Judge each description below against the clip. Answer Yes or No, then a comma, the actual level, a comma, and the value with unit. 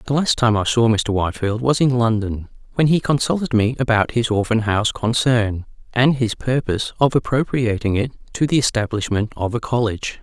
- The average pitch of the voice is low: Yes, low, 115 Hz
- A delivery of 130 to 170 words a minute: No, average, 180 wpm